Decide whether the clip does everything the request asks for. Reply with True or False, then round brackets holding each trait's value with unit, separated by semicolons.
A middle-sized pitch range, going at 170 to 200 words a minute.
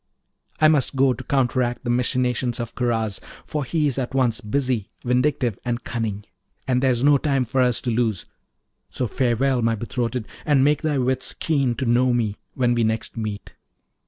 False (2.2 semitones; 175 wpm)